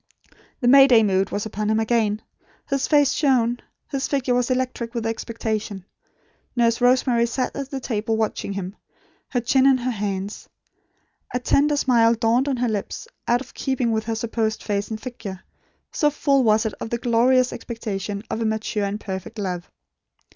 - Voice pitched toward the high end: Yes, high, 230 Hz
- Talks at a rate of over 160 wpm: Yes, average, 175 wpm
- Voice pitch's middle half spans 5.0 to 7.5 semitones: No, average, 3.0 semitones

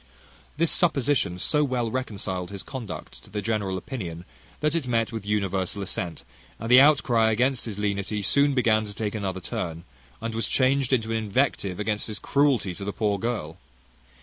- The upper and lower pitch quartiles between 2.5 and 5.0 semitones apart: Yes, average, 4.5 semitones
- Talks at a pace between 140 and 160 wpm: No, average, 175 wpm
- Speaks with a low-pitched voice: Yes, low, 110 Hz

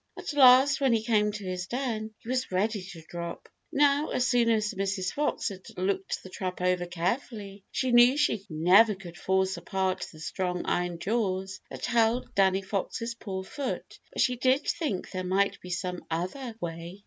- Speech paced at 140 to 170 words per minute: No, average, 185 wpm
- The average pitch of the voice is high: Yes, high, 195 Hz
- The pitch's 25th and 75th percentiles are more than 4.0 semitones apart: Yes, average, 4.6 semitones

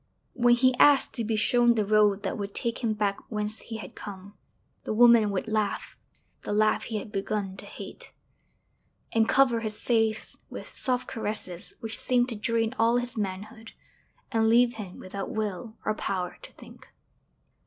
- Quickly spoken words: No, average, 175 wpm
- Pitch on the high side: Yes, high, 220 Hz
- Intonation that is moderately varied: No, narrow, 2.3 semitones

